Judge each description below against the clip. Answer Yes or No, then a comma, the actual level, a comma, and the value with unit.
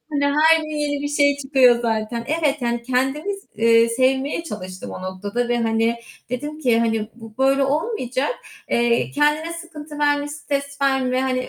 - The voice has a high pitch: Yes, very high, 270 Hz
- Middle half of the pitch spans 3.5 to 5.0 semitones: Yes, average, 3.9 semitones